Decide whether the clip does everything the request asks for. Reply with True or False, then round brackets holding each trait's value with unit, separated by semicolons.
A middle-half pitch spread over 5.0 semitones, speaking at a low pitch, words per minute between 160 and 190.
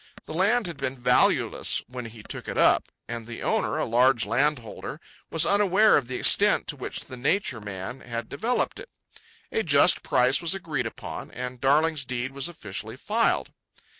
True (5.6 semitones; 130 Hz; 175 wpm)